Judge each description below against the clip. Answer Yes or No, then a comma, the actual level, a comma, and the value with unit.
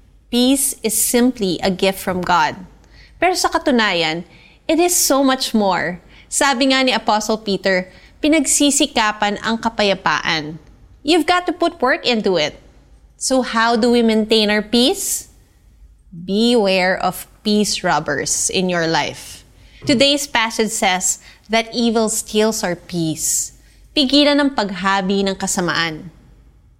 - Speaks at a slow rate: No, average, 130 wpm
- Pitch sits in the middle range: No, high, 220 Hz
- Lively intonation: Yes, wide, 6.0 semitones